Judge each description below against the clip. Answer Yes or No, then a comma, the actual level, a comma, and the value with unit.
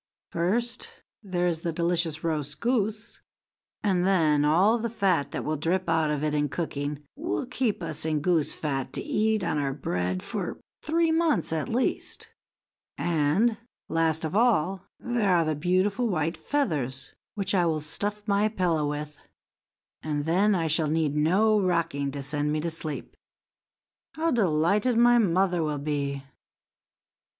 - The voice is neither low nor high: Yes, medium, 170 Hz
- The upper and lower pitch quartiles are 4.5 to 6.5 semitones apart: Yes, wide, 5.6 semitones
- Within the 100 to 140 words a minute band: No, average, 155 wpm